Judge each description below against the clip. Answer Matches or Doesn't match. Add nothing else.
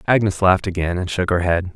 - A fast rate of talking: Matches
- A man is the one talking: Matches